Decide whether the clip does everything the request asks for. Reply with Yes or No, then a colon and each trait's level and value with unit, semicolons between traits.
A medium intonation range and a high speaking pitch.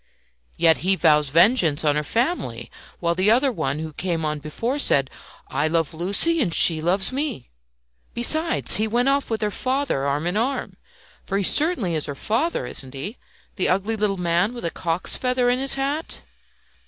No: wide, 7.7 semitones; high, 195 Hz